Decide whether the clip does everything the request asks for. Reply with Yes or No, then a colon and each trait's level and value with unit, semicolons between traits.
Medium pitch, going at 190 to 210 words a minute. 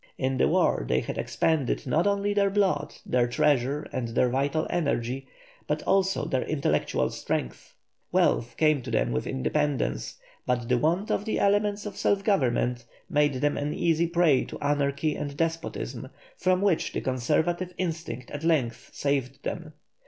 No: medium, 145 Hz; average, 160 wpm